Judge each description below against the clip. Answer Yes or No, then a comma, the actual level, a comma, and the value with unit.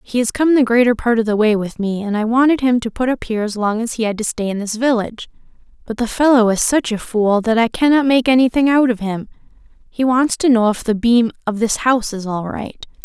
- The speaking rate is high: Yes, fast, 260 wpm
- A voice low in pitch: No, high, 230 Hz